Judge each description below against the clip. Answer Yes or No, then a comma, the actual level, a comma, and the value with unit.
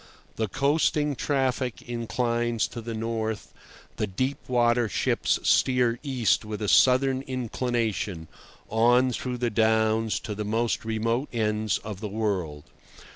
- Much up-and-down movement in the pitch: No, narrow, 2.5 semitones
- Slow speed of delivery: Yes, slow, 130 wpm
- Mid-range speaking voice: No, low, 115 Hz